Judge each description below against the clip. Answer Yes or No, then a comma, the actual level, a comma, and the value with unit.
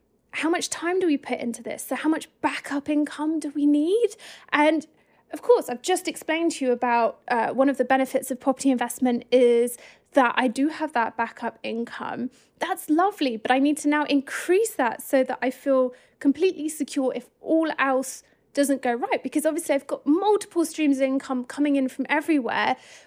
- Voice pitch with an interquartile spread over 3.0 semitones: Yes, average, 3.5 semitones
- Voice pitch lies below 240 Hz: No, very high, 280 Hz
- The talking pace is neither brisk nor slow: Yes, average, 195 wpm